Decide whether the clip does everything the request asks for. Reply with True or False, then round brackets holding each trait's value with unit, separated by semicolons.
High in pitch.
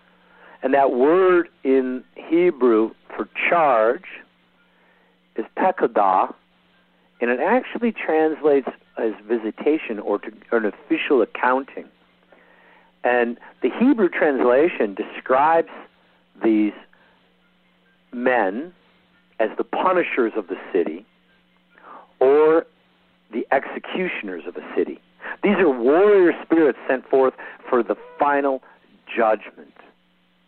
False (135 Hz)